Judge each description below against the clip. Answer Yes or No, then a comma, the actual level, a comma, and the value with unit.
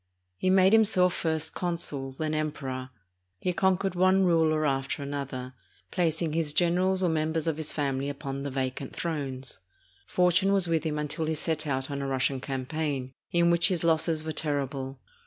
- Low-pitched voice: No, medium, 155 Hz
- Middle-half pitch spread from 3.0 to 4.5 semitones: Yes, average, 3.8 semitones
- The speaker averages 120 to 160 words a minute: No, average, 175 wpm